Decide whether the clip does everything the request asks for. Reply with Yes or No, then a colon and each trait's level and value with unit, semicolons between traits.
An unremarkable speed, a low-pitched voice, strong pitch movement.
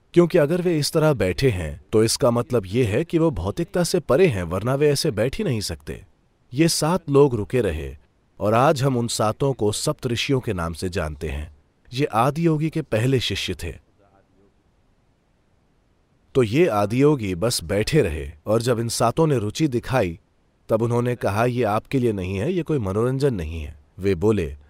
Yes: average, 190 wpm; low, 115 Hz; wide, 6.8 semitones